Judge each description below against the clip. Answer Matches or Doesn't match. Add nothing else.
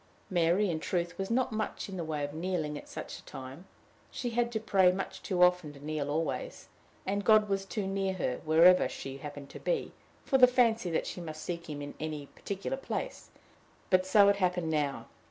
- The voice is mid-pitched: Matches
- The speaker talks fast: Matches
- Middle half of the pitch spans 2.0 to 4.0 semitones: Doesn't match